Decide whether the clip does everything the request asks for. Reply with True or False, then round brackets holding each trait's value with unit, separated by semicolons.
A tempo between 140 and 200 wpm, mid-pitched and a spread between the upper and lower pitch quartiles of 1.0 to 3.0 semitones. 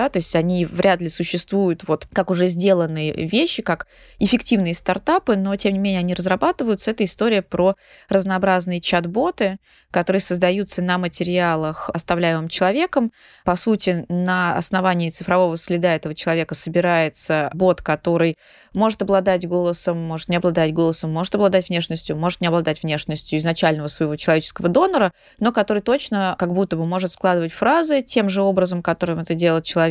True (155 wpm; 180 Hz; 2.6 semitones)